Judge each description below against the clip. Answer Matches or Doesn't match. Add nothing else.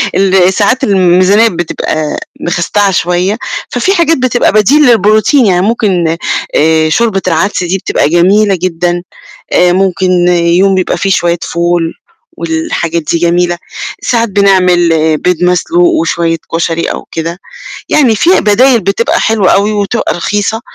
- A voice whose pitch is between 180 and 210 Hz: Matches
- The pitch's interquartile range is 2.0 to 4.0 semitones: Matches